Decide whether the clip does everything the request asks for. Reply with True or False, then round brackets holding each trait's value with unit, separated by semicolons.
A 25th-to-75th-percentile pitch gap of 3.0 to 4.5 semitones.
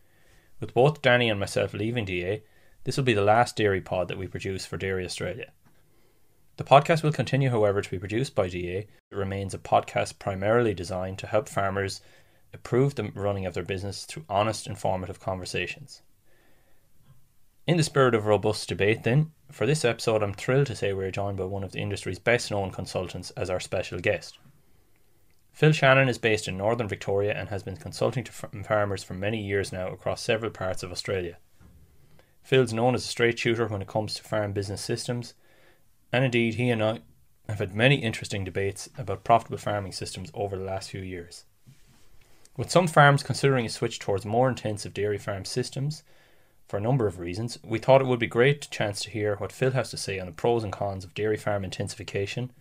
True (4.0 semitones)